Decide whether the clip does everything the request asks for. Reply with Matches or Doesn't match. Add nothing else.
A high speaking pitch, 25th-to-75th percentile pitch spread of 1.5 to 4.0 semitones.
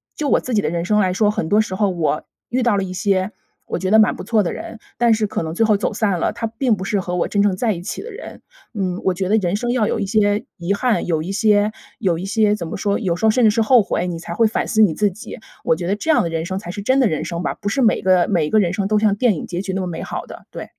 Matches